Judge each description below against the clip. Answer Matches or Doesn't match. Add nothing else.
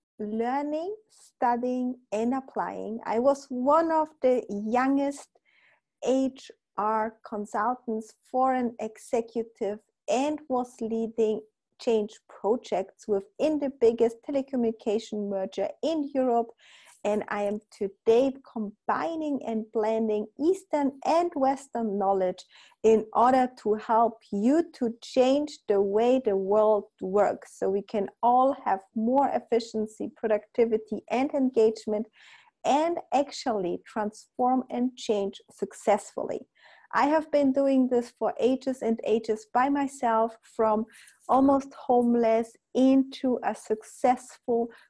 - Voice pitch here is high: Matches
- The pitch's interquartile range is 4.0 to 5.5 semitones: Doesn't match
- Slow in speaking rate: Matches